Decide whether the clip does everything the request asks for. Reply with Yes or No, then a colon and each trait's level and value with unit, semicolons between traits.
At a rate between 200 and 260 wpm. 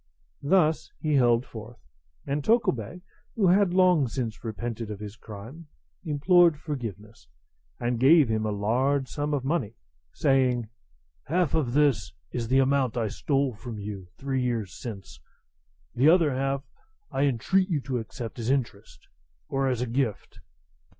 No: average, 150 wpm